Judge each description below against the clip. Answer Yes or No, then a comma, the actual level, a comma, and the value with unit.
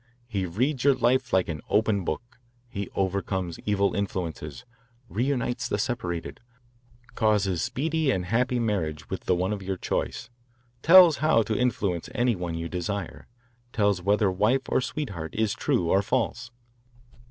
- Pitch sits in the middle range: No, low, 100 Hz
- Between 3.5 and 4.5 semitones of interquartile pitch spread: No, average, 5.1 semitones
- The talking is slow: No, average, 150 wpm